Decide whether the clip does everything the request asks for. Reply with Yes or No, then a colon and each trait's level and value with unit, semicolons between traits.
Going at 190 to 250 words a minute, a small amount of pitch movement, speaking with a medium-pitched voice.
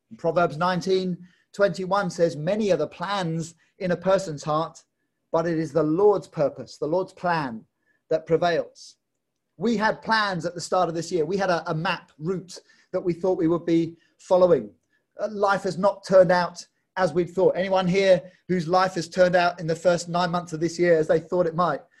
Yes: average, 200 wpm; narrow, 2.1 semitones; medium, 180 Hz